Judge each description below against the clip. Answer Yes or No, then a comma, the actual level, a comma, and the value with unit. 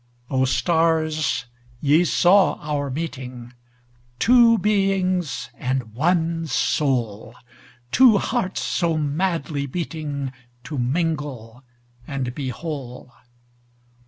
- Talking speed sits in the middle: No, slow, 75 wpm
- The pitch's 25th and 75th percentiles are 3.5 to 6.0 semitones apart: Yes, average, 5.1 semitones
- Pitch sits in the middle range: Yes, medium, 145 Hz